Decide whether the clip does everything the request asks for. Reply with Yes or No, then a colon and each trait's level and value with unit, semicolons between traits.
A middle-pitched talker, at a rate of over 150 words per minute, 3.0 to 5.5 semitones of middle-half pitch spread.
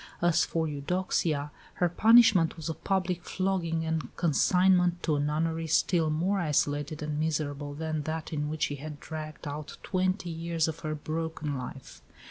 No: medium, 160 Hz; average, 160 wpm; narrow, 2.5 semitones